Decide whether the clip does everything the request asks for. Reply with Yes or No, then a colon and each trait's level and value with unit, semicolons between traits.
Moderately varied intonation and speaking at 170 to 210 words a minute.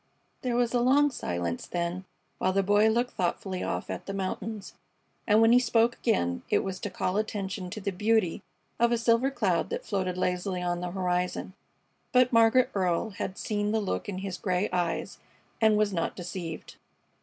Yes: average, 3.9 semitones; average, 185 wpm